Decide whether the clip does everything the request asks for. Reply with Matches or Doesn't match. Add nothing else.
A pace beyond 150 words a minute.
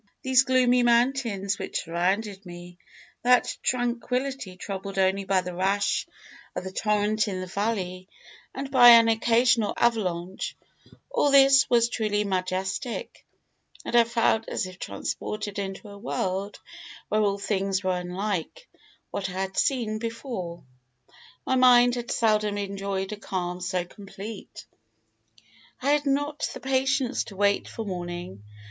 Doesn't match